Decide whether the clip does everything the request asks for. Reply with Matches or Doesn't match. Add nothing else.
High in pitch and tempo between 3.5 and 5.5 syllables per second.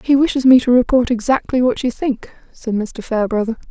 Doesn't match